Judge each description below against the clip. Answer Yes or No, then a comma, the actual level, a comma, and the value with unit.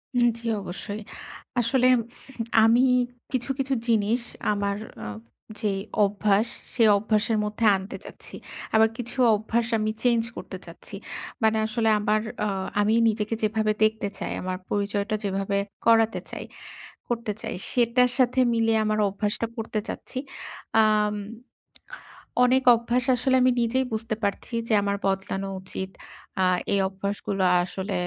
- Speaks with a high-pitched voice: Yes, high, 215 Hz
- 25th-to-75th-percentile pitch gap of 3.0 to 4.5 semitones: No, narrow, 2.5 semitones